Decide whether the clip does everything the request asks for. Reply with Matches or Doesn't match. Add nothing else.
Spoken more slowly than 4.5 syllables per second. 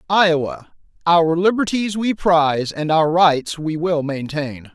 Matches